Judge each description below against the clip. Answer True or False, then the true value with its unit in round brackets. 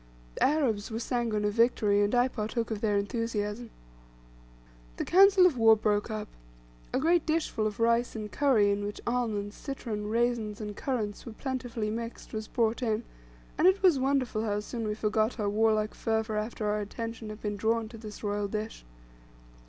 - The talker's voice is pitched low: False (220 Hz)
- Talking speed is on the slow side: False (180 wpm)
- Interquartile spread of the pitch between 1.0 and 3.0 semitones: True (2.4 semitones)